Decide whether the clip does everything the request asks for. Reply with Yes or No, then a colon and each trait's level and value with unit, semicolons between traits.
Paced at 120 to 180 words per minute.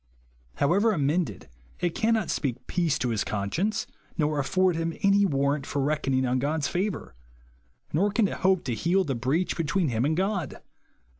Yes: average, 170 wpm